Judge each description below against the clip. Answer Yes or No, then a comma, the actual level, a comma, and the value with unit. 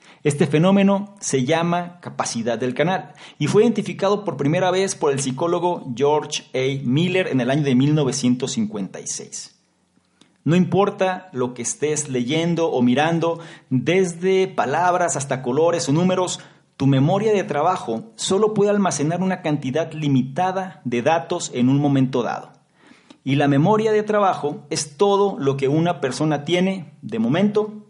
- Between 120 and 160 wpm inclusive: Yes, average, 145 wpm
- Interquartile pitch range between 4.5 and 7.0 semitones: Yes, average, 5.3 semitones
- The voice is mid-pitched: Yes, medium, 165 Hz